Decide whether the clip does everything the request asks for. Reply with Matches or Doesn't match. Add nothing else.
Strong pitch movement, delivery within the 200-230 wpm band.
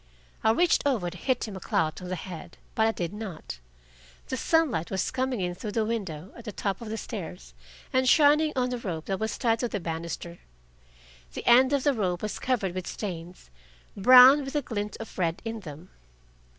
Matches